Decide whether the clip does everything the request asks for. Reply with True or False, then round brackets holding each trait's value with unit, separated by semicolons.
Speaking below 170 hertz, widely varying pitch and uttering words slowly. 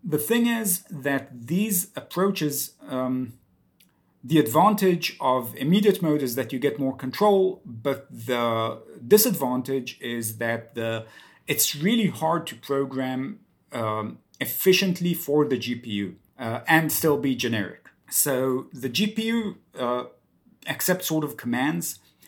True (140 Hz; 6.9 semitones; 125 wpm)